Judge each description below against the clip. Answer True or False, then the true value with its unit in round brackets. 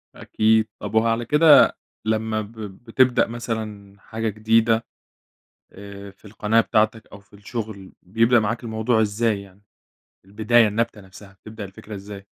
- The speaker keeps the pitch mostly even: True (2.0 semitones)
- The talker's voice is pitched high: False (110 Hz)